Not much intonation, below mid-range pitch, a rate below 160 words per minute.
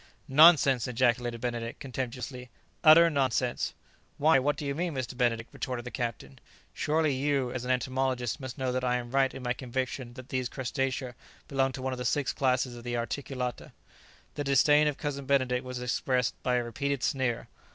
No: narrow, 2.0 semitones; low, 130 Hz; average, 185 wpm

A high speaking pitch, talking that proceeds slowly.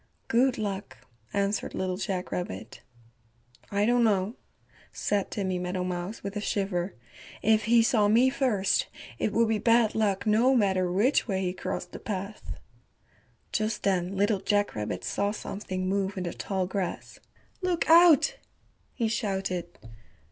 No: high, 200 Hz; average, 145 wpm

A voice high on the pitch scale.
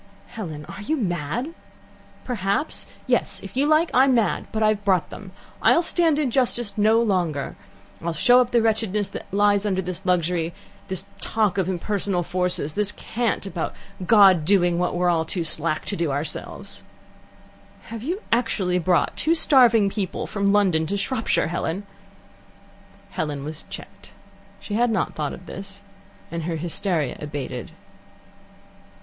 Yes: high, 195 Hz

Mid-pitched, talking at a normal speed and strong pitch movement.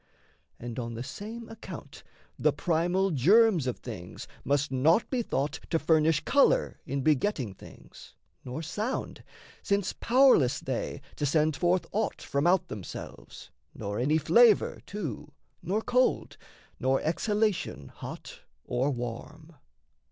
No: medium, 155 Hz; slow, 130 wpm; wide, 7.7 semitones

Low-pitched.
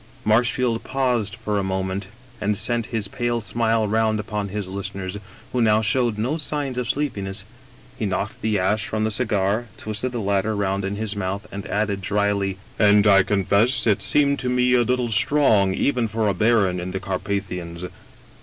Yes: low, 105 Hz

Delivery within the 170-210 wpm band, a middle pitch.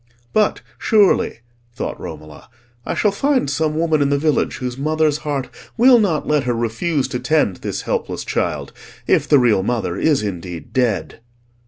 No: average, 160 wpm; medium, 145 Hz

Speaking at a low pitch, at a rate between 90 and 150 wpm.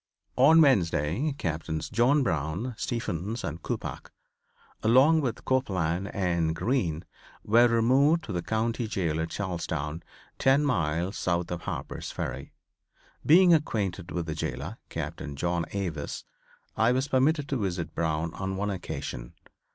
Yes: very low, 95 Hz; slow, 135 wpm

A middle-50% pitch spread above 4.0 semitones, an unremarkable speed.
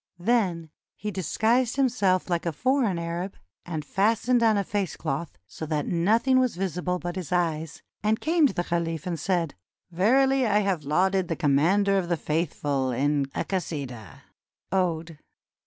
Yes: average, 4.4 semitones; average, 165 wpm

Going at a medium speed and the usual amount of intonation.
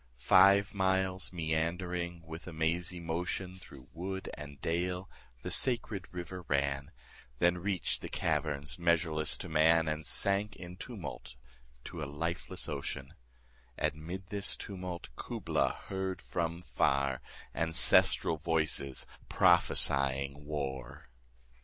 No: slow, 120 wpm; average, 3.2 semitones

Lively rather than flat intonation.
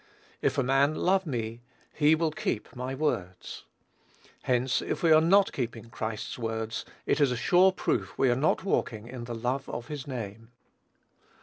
No: average, 4.8 semitones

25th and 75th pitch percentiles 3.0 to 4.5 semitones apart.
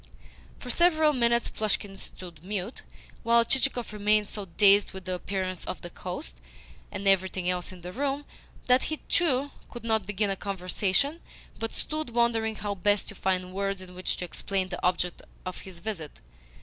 Yes: average, 4.2 semitones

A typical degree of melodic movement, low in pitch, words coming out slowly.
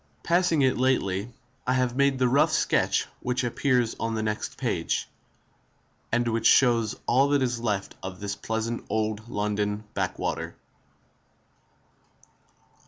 Yes: average, 3.3 semitones; low, 120 Hz; slow, 120 wpm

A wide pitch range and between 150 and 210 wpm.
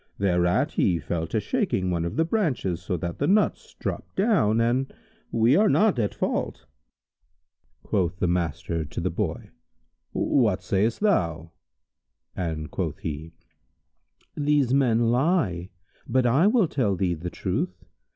No: wide, 7.9 semitones; average, 140 wpm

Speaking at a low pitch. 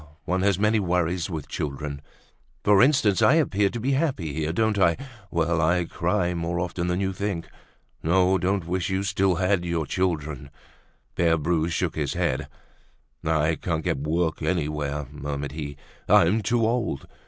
Yes: very low, 85 Hz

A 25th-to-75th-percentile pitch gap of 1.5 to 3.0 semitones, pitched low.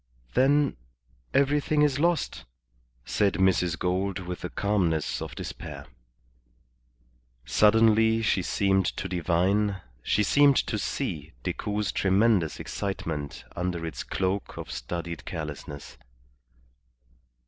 No: average, 4.3 semitones; very low, 95 Hz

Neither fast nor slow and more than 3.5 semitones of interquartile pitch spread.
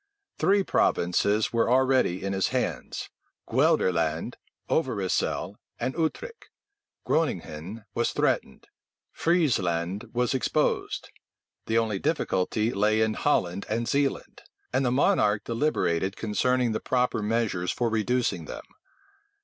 No: slow, 110 wpm; average, 4.6 semitones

